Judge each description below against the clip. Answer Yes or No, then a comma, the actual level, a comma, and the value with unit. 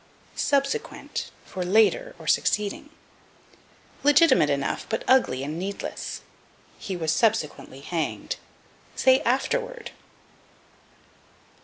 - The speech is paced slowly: Yes, slow, 90 wpm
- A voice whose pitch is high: Yes, high, 220 Hz